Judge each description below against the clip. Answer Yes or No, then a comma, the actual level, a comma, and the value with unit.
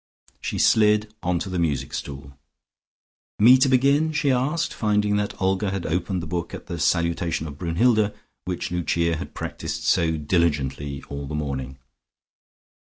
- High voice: No, very low, 85 Hz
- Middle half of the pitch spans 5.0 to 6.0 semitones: Yes, average, 5.3 semitones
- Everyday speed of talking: Yes, average, 150 wpm